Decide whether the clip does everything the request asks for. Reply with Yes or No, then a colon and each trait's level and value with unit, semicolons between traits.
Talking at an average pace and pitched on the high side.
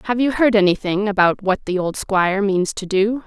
No: fast, 220 wpm; high, 200 Hz